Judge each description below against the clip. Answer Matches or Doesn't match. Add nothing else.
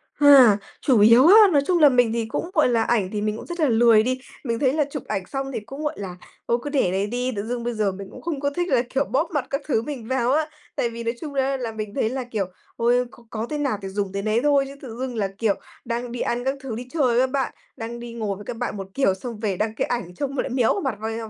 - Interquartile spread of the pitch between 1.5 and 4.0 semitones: Matches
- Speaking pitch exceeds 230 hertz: Matches